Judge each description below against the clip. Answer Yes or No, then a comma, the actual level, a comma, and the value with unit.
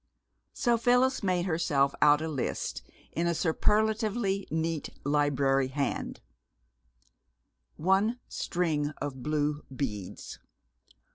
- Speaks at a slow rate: Yes, slow, 95 wpm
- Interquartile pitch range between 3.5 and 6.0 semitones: Yes, average, 5.3 semitones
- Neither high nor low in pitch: Yes, medium, 160 Hz